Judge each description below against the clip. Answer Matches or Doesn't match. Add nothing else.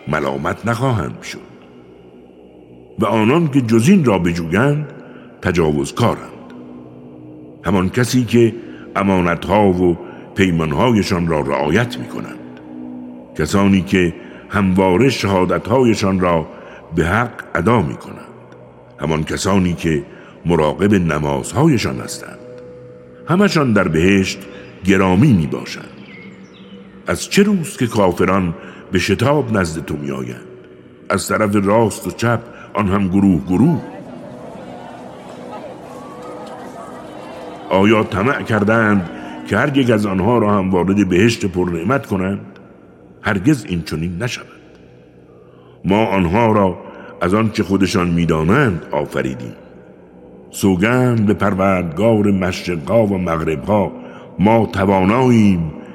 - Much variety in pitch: Matches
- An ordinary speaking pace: Doesn't match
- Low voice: Matches